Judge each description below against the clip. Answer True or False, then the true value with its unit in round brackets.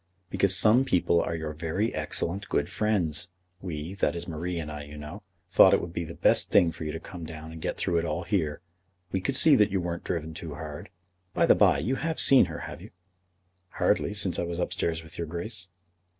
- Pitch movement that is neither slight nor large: True (3.1 semitones)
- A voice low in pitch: True (85 Hz)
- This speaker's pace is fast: True (230 wpm)